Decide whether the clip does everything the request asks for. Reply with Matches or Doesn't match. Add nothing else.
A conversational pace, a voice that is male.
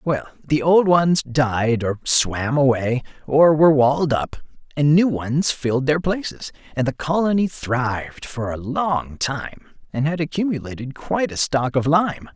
Matches